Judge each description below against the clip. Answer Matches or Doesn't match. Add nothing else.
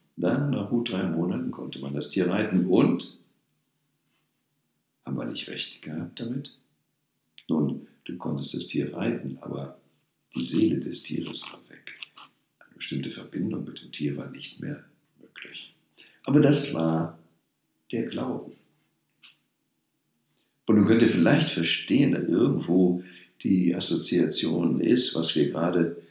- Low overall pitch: Matches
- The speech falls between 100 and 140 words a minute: Matches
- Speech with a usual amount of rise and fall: Matches